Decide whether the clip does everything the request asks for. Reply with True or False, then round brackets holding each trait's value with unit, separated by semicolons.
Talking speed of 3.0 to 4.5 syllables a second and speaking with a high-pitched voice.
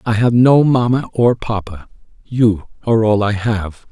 False (4.3 syllables/s; 110 Hz)